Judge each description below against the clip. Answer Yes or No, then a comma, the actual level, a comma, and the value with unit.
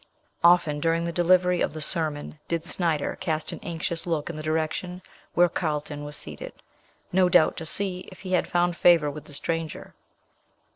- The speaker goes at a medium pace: Yes, average, 180 wpm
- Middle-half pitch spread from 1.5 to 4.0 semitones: Yes, narrow, 2.4 semitones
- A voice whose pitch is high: No, medium, 165 Hz